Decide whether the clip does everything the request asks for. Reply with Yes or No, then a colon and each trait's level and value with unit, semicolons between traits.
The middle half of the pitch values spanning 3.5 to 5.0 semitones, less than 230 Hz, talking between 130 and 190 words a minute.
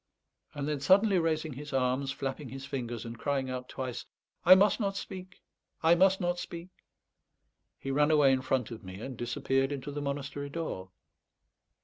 Yes: average, 4.1 semitones; medium, 140 Hz; average, 170 wpm